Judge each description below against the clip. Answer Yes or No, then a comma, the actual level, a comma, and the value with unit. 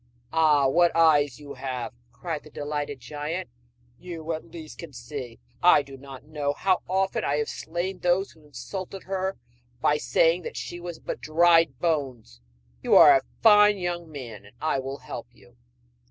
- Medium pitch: Yes, medium, 155 Hz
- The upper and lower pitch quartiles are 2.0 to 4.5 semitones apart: Yes, average, 4.1 semitones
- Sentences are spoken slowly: No, average, 170 wpm